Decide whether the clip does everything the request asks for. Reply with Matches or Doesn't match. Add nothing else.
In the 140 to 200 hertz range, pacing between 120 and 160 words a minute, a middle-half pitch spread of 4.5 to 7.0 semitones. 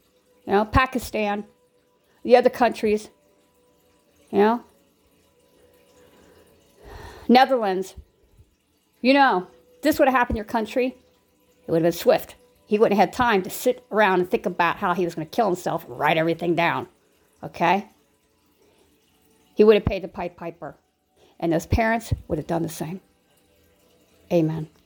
Matches